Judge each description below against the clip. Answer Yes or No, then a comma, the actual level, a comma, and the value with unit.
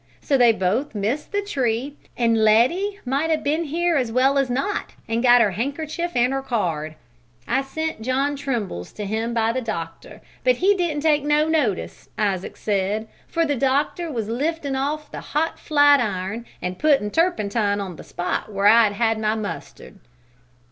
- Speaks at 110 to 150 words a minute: No, average, 175 wpm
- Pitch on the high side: Yes, very high, 250 Hz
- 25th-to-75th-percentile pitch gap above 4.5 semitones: Yes, wide, 5.6 semitones